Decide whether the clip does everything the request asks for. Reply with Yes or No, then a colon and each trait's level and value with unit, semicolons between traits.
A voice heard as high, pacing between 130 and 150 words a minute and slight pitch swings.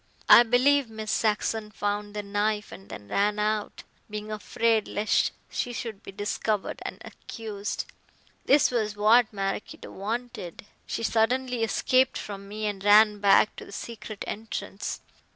Yes: high, 215 Hz; average, 145 wpm; narrow, 1.7 semitones